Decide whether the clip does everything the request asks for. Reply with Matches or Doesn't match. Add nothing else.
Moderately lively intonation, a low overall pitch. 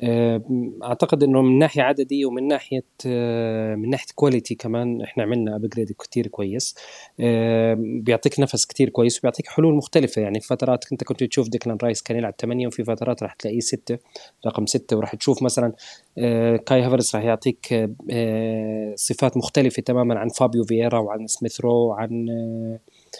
Doesn't match